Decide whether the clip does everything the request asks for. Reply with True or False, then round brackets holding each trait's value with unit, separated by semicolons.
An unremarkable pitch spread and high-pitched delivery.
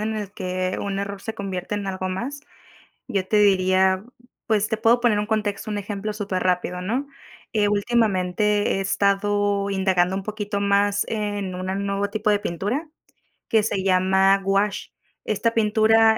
False (1.9 semitones; 200 Hz)